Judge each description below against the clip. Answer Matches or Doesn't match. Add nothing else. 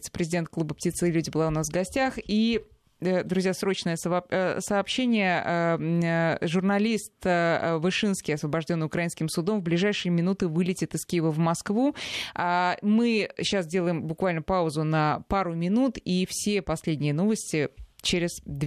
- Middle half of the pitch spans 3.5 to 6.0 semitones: Doesn't match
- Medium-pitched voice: Matches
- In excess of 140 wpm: Doesn't match